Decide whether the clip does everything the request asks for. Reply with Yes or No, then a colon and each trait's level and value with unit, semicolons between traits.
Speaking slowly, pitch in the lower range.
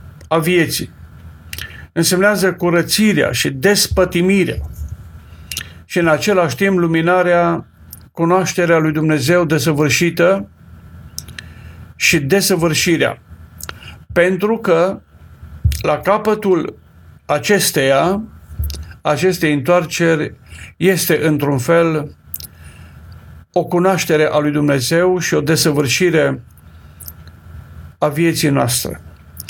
No: slow, 75 wpm; medium, 150 Hz